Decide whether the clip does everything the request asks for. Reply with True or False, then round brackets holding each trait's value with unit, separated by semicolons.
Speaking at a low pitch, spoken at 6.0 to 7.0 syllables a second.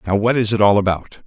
True (105 Hz; 6.4 syllables/s)